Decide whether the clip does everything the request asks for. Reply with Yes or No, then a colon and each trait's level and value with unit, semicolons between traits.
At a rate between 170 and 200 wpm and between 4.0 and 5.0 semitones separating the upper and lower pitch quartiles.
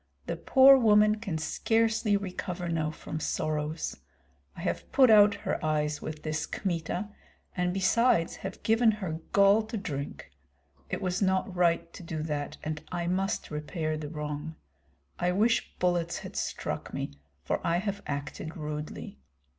No: average, 155 wpm; average, 4.7 semitones